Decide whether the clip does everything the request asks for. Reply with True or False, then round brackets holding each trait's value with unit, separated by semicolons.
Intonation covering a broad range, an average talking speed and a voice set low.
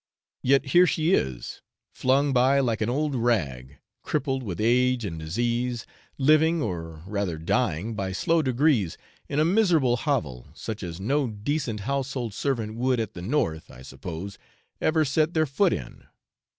True (6.7 semitones; 155 wpm; 120 Hz)